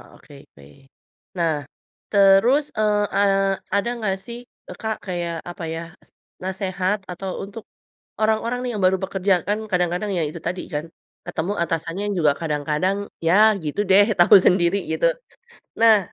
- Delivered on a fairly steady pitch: No, average, 3.2 semitones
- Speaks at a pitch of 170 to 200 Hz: Yes, high, 190 Hz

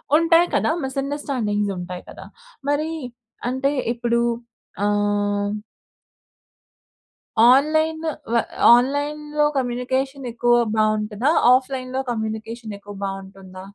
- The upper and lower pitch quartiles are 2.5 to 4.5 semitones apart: No, average, 5.2 semitones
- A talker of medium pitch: No, high, 240 Hz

